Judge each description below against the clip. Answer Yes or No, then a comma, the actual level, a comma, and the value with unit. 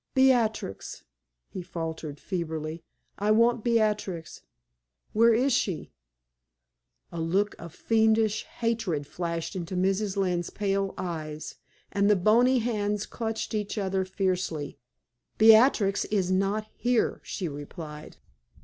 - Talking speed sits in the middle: No, slow, 115 wpm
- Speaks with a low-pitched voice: No, high, 195 Hz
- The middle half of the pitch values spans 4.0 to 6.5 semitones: Yes, average, 4.3 semitones